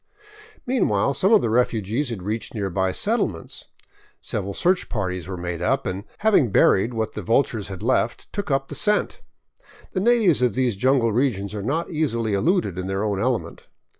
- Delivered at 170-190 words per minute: Yes, average, 175 wpm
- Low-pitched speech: Yes, low, 115 Hz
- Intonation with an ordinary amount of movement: No, wide, 6.3 semitones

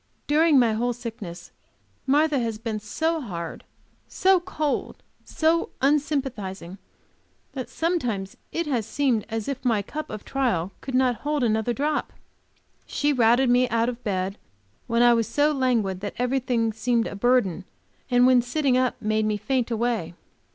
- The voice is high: Yes, high, 245 Hz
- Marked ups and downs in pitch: No, average, 4.0 semitones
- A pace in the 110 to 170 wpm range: Yes, average, 155 wpm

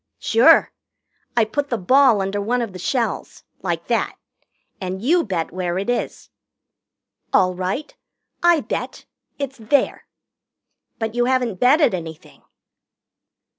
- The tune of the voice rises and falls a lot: Yes, wide, 6.1 semitones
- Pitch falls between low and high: No, high, 230 Hz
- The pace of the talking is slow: Yes, slow, 130 wpm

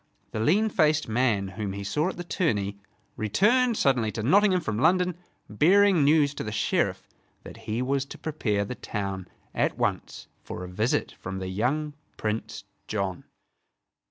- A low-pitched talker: Yes, low, 125 Hz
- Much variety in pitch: Yes, wide, 7.6 semitones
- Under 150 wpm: No, average, 160 wpm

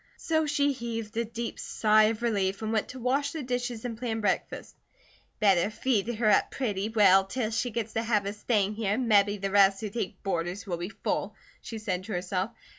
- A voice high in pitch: Yes, high, 215 Hz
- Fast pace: Yes, fast, 210 wpm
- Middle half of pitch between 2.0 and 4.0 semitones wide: Yes, average, 2.9 semitones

